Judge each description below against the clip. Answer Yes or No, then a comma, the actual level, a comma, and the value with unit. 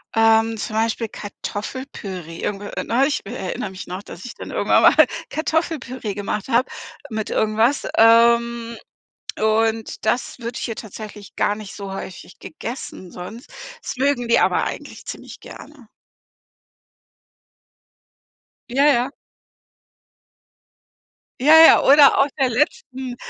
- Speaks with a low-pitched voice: No, high, 230 Hz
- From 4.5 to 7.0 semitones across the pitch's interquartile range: No, average, 3.4 semitones